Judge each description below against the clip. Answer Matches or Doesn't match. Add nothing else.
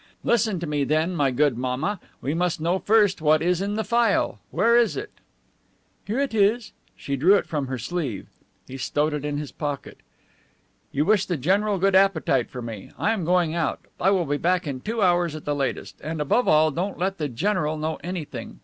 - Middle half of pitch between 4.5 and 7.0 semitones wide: Matches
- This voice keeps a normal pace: Doesn't match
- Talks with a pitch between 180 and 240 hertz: Doesn't match